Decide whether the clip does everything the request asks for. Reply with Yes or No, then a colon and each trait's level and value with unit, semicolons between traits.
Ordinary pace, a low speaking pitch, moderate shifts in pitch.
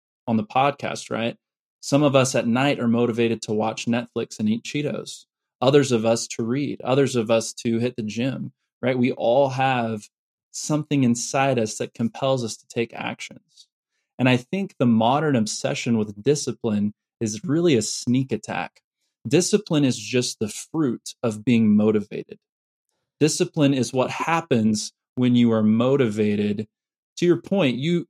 Yes: average, 160 wpm; low, 125 Hz; average, 3.6 semitones